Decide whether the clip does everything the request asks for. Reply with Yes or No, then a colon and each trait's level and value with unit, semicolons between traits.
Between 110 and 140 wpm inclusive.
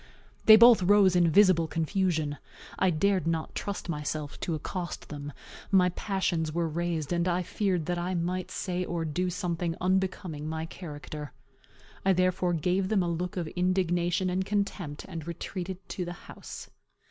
No: average, 160 wpm